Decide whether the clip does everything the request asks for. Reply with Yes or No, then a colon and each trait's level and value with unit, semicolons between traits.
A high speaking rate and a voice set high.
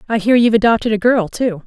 Yes: fast, 250 wpm; high, 220 Hz